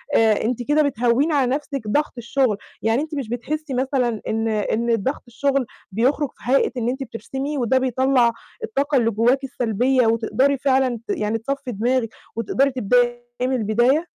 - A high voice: Yes, very high, 250 Hz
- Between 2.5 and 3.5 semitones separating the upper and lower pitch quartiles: Yes, average, 3.1 semitones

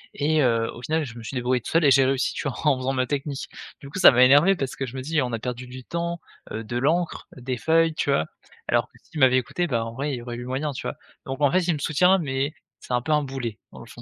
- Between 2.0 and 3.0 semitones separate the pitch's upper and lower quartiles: No, average, 3.4 semitones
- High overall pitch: No, low, 135 Hz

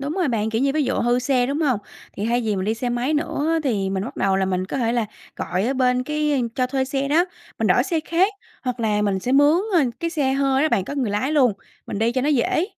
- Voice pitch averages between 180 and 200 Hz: No, very high, 255 Hz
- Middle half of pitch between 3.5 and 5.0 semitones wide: Yes, average, 4.5 semitones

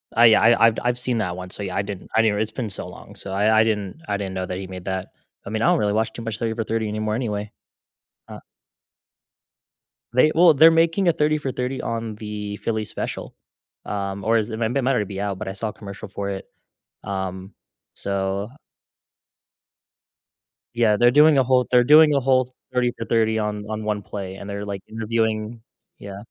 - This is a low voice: Yes, low, 110 Hz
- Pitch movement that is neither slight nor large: Yes, average, 3.0 semitones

